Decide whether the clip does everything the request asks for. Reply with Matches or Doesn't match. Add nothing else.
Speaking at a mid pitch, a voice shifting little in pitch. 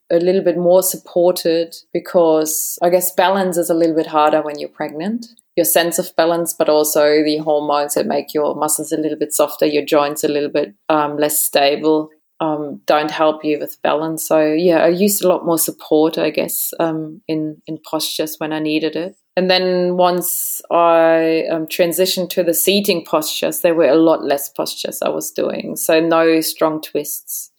Matches